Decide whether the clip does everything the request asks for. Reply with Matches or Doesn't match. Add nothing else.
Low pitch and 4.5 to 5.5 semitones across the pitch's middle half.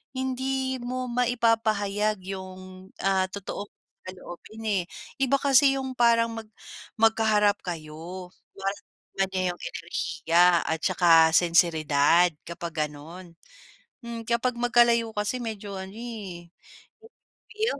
Doesn't match